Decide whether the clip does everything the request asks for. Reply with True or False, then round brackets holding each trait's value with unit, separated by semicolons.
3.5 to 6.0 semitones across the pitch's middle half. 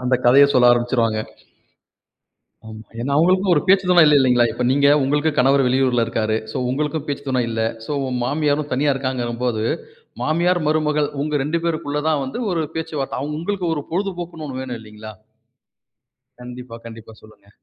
True (4.2 semitones)